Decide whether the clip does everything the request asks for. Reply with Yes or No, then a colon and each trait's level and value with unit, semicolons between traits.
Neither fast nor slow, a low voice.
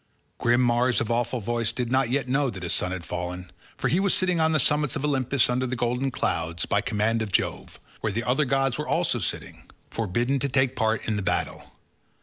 No: fast, 220 wpm; low, 120 Hz